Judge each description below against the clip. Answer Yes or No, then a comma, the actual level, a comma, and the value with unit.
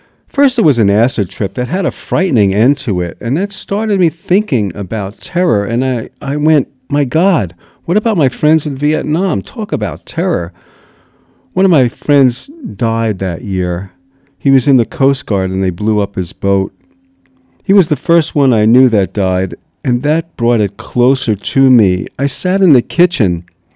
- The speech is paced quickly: No, average, 190 wpm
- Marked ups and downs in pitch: Yes, wide, 7.3 semitones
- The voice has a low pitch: Yes, low, 125 Hz